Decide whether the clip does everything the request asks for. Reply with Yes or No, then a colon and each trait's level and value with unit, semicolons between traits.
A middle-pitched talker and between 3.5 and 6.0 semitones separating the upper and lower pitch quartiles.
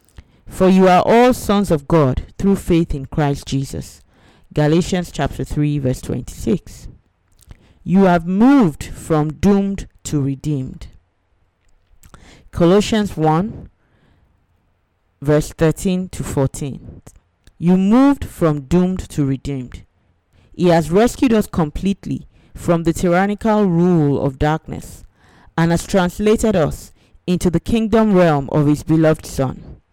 Yes: medium, 160 Hz; wide, 5.6 semitones